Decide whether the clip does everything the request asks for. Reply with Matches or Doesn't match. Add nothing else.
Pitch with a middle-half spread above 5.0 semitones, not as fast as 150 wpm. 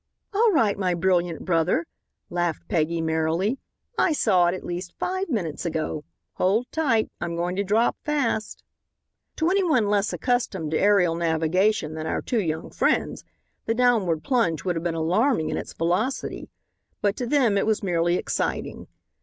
Doesn't match